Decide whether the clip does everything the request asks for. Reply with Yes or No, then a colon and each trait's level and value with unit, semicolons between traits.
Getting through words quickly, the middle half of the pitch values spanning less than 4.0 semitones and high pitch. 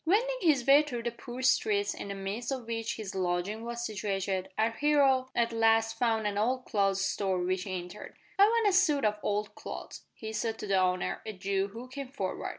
No: fast, 215 wpm; average, 4.5 semitones; high, 225 Hz